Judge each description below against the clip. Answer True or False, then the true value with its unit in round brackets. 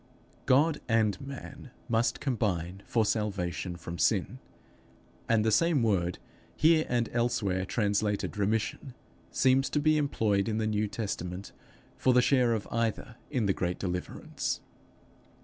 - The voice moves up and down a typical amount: True (4.4 semitones)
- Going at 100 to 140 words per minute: True (135 wpm)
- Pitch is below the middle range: True (110 Hz)